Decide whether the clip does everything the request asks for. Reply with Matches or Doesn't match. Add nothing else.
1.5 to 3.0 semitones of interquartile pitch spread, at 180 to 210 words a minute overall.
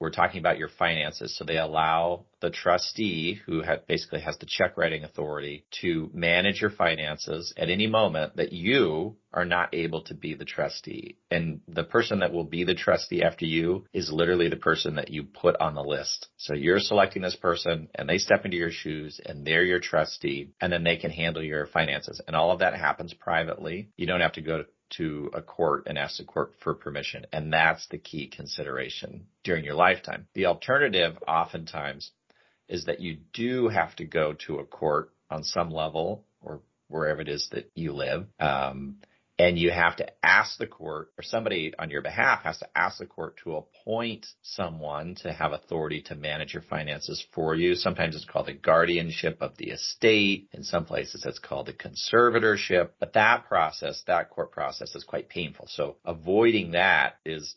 Matches